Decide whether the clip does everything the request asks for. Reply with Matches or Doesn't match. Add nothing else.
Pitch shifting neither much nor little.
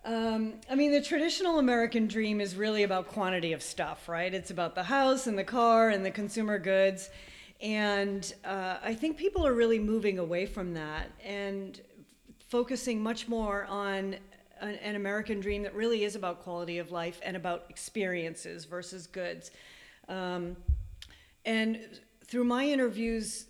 Matches